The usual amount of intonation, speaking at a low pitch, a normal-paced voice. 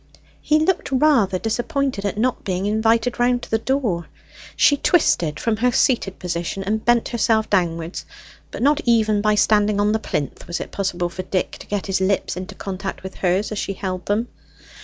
No: average, 4.1 semitones; high, 210 Hz; average, 190 wpm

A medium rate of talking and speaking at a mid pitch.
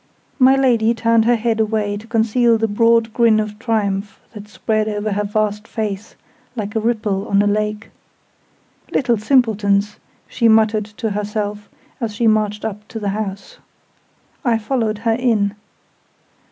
No: average, 155 wpm; high, 215 Hz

